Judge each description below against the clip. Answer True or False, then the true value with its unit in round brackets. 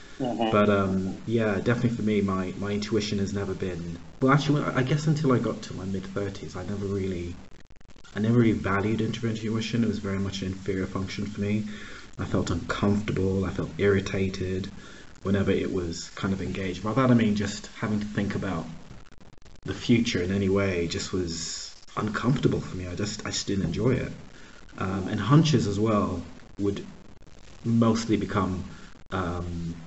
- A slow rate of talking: False (175 wpm)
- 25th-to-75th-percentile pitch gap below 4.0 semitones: True (2.6 semitones)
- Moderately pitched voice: False (100 Hz)